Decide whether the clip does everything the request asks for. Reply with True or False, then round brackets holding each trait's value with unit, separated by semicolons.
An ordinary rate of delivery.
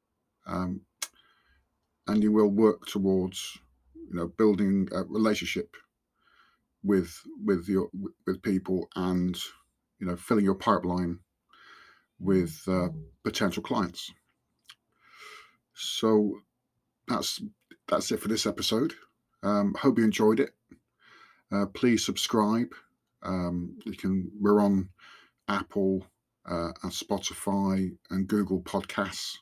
False (110 wpm)